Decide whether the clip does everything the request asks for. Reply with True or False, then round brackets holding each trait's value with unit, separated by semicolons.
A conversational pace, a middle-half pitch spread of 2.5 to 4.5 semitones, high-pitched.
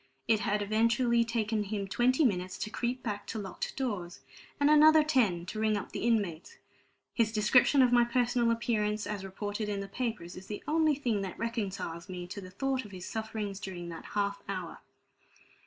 True (190 wpm; 3.4 semitones; 215 Hz)